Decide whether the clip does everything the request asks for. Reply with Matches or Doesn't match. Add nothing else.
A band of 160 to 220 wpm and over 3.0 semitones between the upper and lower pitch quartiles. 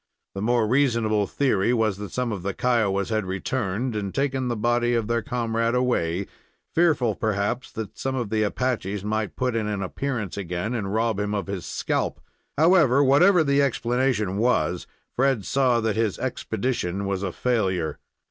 Matches